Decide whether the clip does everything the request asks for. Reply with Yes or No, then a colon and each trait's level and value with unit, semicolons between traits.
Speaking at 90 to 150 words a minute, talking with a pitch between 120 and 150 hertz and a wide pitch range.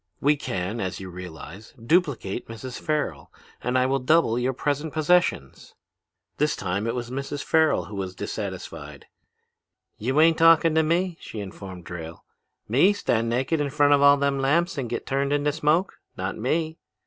No: average, 170 wpm; low, 135 Hz; wide, 6.5 semitones